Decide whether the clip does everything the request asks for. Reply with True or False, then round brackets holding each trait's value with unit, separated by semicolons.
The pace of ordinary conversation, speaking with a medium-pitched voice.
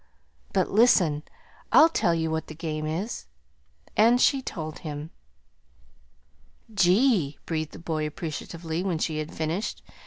False (130 wpm; 165 Hz)